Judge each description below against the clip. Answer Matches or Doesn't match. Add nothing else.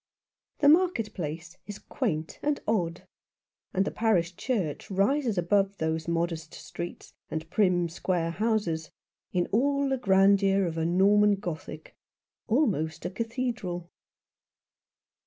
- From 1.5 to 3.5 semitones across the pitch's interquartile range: Doesn't match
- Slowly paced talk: Matches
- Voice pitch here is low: Doesn't match